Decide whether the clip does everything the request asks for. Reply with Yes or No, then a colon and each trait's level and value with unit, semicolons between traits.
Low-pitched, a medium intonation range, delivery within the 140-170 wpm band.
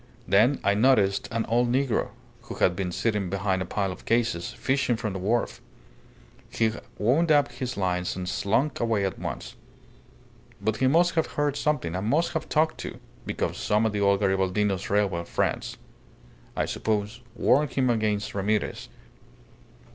Yes: low, 110 Hz; average, 4.6 semitones; average, 160 wpm